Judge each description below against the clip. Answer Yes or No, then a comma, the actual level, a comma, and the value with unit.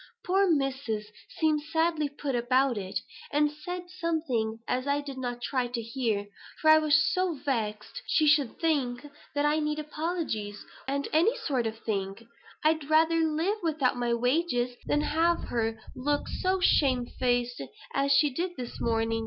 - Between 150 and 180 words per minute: Yes, average, 160 wpm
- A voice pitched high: Yes, very high, 280 Hz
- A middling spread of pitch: Yes, average, 4.5 semitones